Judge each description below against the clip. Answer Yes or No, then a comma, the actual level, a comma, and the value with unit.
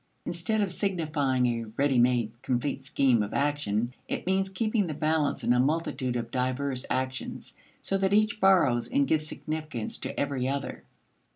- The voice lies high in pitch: No, medium, 140 Hz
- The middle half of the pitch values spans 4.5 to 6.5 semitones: Yes, wide, 5.5 semitones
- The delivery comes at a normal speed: Yes, average, 165 wpm